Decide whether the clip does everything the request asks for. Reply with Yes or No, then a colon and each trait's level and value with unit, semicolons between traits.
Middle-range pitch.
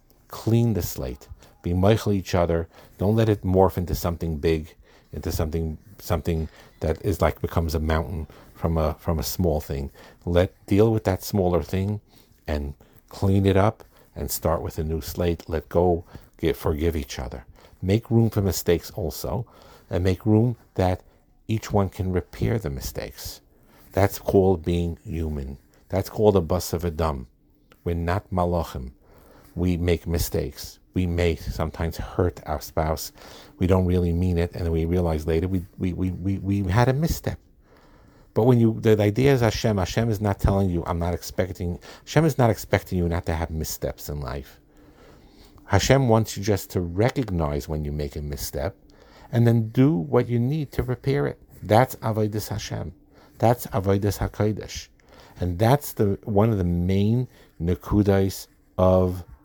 No: very low, 90 Hz